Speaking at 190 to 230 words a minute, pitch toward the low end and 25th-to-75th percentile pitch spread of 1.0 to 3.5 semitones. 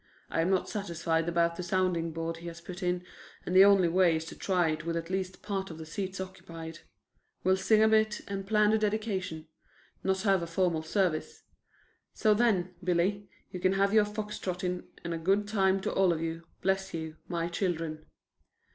No: average, 200 wpm; medium, 185 Hz; average, 2.8 semitones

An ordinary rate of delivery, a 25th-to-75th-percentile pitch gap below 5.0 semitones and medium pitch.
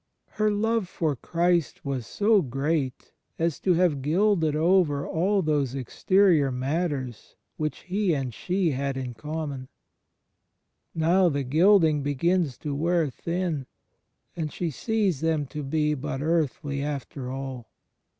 No: slow, 130 wpm; average, 4.3 semitones; medium, 155 Hz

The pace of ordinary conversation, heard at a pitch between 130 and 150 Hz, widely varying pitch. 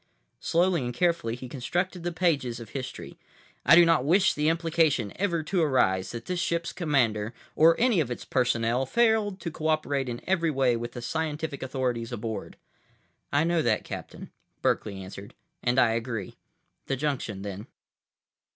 Yes: average, 160 wpm; medium, 140 Hz; wide, 6.0 semitones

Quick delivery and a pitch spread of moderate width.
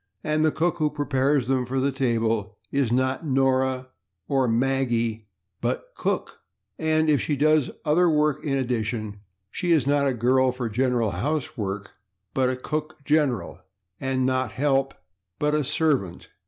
No: average, 155 wpm; average, 3.4 semitones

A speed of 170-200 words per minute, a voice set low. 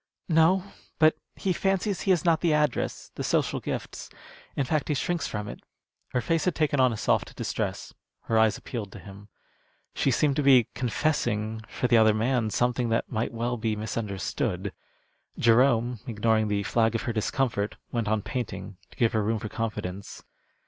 Yes: average, 180 wpm; low, 120 Hz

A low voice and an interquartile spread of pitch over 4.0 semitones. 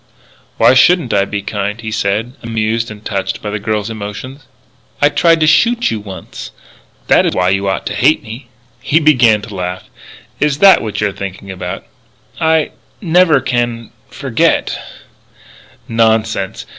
Yes: low, 110 Hz; average, 5.2 semitones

